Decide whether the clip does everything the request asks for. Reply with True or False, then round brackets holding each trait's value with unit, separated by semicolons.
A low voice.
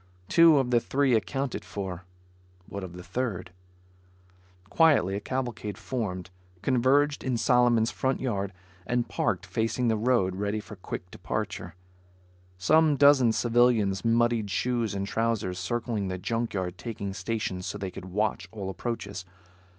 True (110 Hz)